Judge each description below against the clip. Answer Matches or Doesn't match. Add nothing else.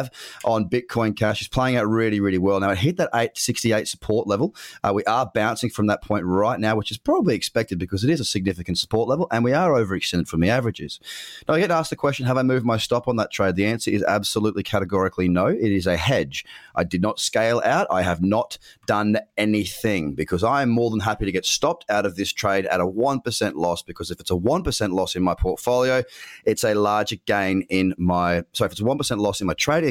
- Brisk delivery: Matches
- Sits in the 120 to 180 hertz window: Doesn't match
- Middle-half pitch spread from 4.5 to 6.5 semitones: Doesn't match